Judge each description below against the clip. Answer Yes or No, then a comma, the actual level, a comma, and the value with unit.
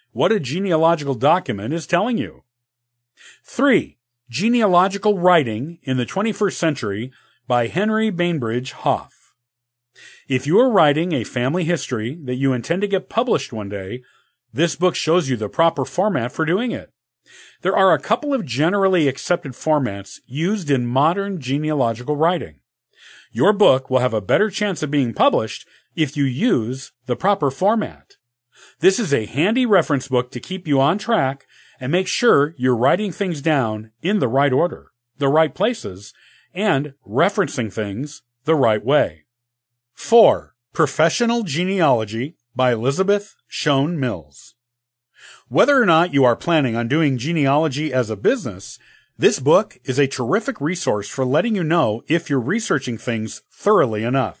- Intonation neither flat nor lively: No, wide, 6.2 semitones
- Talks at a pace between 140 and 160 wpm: Yes, average, 150 wpm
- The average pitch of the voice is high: No, medium, 145 Hz